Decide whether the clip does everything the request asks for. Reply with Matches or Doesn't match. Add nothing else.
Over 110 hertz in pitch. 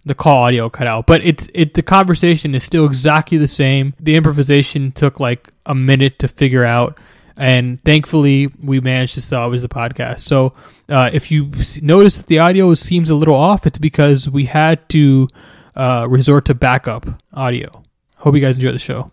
Matches